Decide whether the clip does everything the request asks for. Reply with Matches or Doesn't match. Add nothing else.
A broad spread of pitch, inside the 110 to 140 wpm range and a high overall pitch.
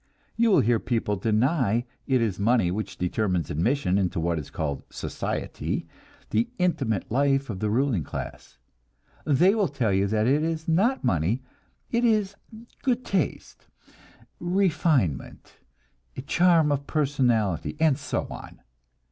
Doesn't match